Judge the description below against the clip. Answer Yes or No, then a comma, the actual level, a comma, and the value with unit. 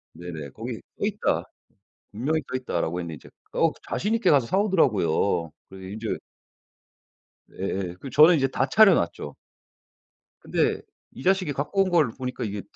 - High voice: No, low, 125 Hz